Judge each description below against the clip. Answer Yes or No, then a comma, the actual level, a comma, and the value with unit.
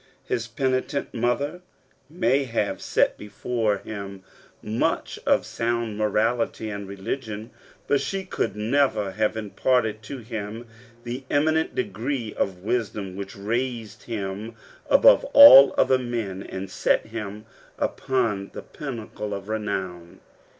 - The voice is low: Yes, low, 110 Hz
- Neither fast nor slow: No, slow, 120 wpm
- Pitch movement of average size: Yes, average, 3.6 semitones